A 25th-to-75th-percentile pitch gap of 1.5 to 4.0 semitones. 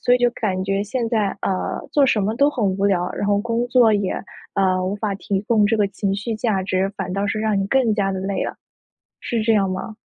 Yes: average, 2.7 semitones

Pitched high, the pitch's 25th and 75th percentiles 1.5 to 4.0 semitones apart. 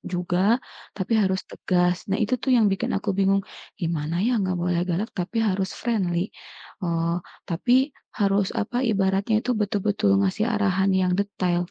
Yes: high, 195 Hz; average, 2.8 semitones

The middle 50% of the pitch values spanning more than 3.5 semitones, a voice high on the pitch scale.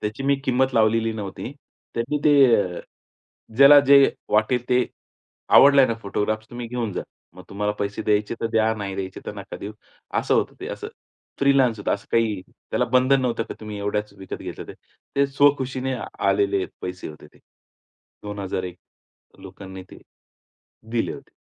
No: average, 4.2 semitones; low, 110 Hz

